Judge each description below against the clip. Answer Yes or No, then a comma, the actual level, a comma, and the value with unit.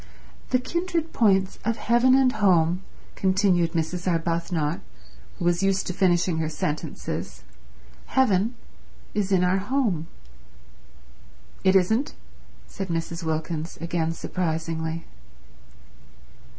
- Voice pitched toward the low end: No, medium, 180 Hz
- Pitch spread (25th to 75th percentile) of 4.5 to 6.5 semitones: No, average, 3.7 semitones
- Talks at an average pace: No, slow, 105 wpm